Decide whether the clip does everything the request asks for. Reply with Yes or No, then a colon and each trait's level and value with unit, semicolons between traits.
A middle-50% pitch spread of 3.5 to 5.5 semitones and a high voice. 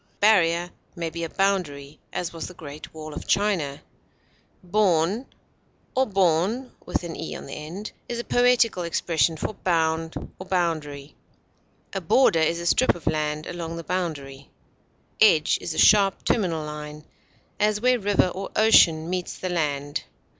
No: average, 4.0 semitones; medium, 170 Hz